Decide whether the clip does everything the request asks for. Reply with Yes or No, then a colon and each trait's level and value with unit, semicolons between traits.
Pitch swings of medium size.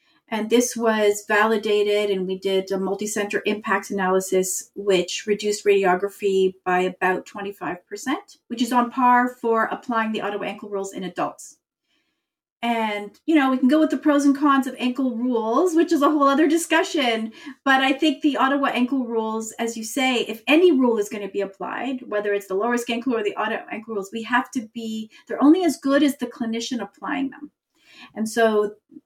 Yes: average, 4.9 semitones